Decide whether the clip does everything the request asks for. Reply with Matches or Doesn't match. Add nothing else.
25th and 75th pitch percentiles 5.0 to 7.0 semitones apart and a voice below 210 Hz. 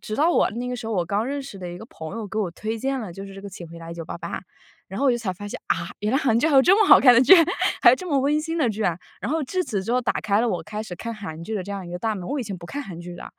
Doesn't match